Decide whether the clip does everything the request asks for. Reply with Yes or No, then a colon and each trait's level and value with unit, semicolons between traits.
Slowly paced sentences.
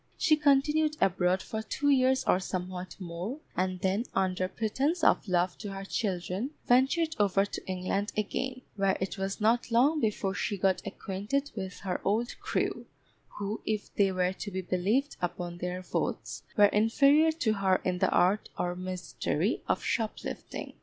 No: average, 165 wpm